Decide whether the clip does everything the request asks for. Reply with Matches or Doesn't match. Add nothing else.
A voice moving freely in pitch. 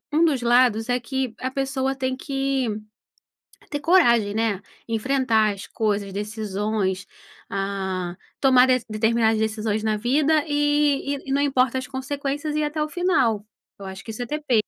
Doesn't match